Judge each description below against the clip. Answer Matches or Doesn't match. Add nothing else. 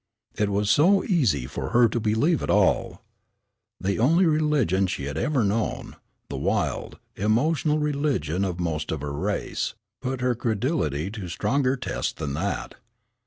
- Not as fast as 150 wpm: Doesn't match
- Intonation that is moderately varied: Doesn't match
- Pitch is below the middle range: Matches